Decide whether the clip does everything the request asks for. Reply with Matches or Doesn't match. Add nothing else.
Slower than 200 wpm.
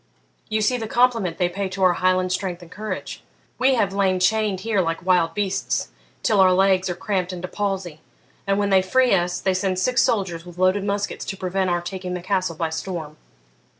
Doesn't match